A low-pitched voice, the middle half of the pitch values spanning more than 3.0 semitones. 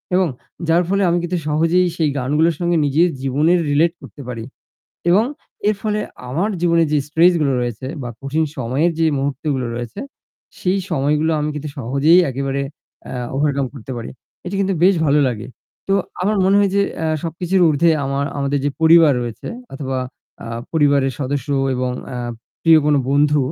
No: medium, 150 Hz; average, 4.0 semitones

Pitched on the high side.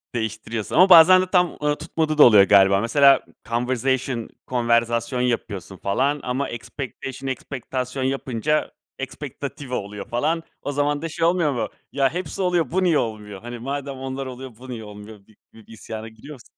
No: low, 130 Hz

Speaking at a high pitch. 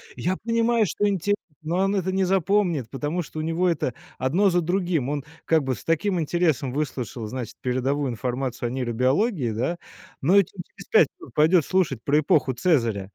No: medium, 155 Hz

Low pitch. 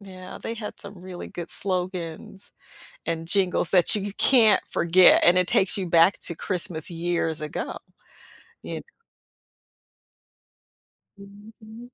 No: medium, 185 Hz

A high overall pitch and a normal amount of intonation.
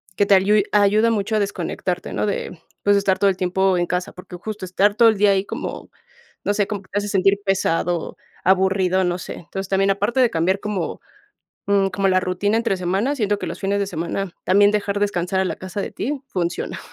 No: high, 195 Hz; narrow, 1.8 semitones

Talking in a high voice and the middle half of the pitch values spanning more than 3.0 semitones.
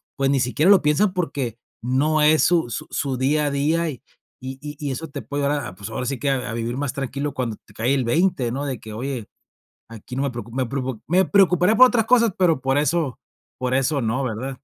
No: low, 135 Hz; average, 3.5 semitones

